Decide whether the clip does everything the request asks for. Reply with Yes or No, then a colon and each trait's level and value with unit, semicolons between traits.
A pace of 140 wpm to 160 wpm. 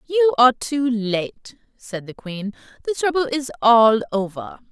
Yes: average, 155 wpm